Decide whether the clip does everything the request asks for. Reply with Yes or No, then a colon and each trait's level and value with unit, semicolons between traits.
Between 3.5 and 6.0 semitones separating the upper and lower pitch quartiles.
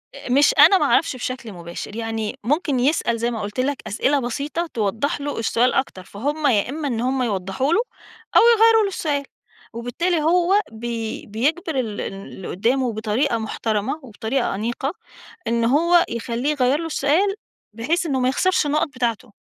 Yes: average, 4.8 semitones